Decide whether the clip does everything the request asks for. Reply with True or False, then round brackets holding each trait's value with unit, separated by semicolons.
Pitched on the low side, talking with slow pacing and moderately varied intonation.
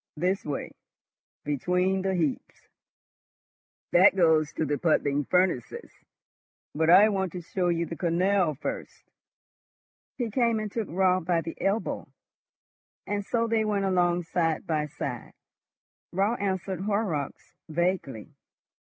False (180 Hz; 125 wpm; 3.4 semitones)